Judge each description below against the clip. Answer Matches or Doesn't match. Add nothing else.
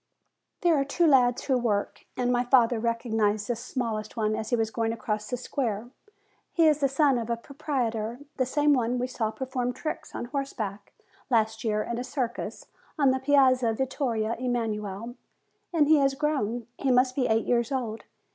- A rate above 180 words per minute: Matches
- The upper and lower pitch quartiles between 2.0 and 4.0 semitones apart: Matches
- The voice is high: Matches